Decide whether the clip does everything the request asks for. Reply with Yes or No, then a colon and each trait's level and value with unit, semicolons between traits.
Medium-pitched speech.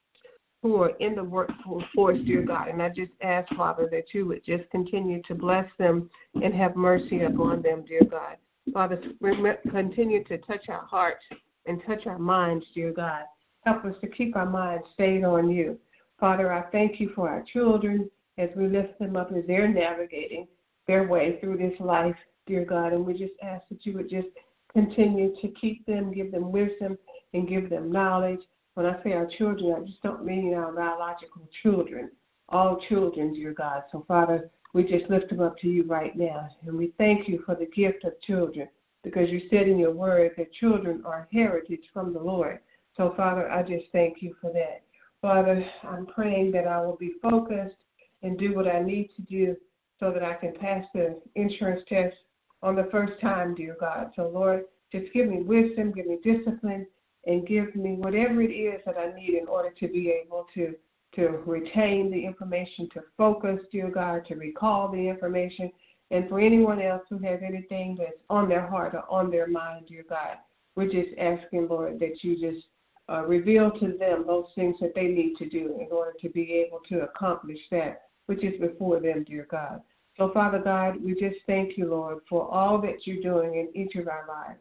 Yes: medium, 180 Hz